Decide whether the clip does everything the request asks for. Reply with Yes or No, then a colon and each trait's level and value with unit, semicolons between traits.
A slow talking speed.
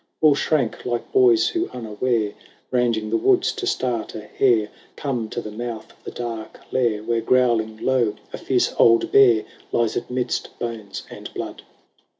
No: average, 160 wpm